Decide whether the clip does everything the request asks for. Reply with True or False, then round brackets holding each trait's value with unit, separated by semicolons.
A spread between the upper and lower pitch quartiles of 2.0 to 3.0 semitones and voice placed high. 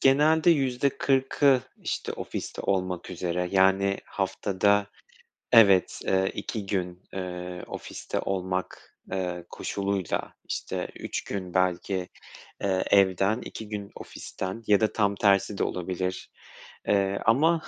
False (2.6 semitones; 95 Hz)